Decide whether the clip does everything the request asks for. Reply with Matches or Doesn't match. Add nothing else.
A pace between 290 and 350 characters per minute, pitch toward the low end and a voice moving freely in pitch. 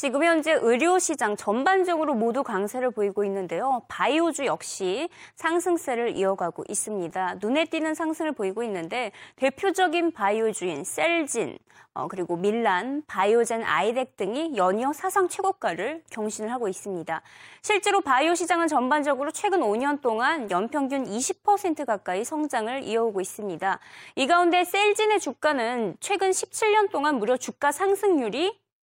Doesn't match